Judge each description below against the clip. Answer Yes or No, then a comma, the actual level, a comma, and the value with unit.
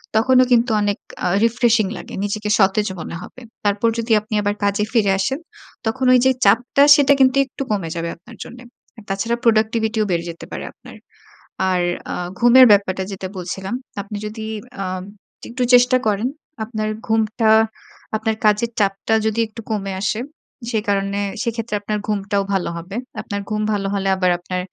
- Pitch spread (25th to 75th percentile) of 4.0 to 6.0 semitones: No, average, 2.8 semitones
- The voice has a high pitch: Yes, high, 215 Hz